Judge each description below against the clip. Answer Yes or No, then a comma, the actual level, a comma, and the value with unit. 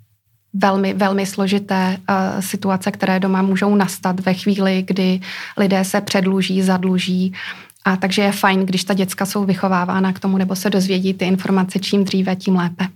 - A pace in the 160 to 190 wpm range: Yes, average, 165 wpm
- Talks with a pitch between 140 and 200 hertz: Yes, high, 190 Hz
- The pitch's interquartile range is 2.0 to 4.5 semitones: No, narrow, 0.8 semitones